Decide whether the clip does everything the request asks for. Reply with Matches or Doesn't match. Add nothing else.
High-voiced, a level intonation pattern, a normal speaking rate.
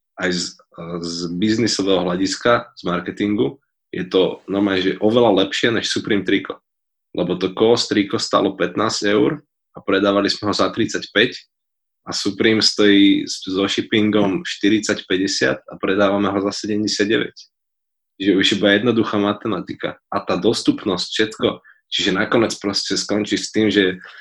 Doesn't match